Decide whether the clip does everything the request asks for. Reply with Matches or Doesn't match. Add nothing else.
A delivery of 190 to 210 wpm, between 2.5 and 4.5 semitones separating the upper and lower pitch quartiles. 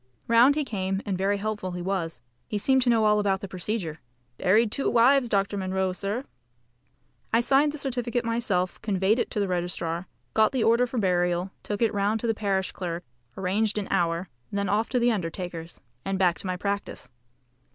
Matches